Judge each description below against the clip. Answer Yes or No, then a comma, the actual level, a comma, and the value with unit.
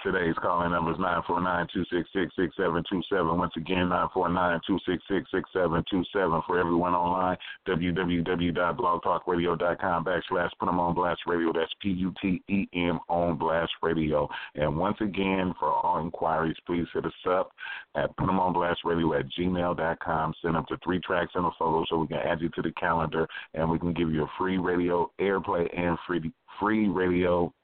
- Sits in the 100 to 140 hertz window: No, very low, 85 Hz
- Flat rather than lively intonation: Yes, narrow, 1.6 semitones